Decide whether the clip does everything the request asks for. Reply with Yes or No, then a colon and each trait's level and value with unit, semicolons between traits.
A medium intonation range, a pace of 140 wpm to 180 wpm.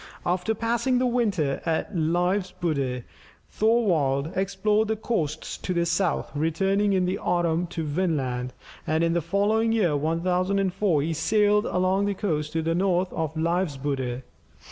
Yes: average, 4.1 semitones; average, 145 wpm